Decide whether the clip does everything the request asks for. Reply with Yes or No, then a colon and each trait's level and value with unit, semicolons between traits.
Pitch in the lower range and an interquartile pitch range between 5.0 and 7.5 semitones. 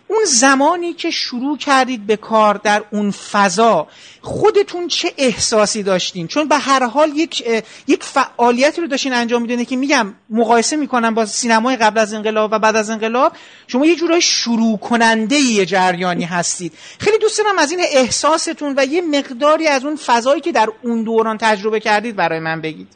No: high, 240 Hz; wide, 5.4 semitones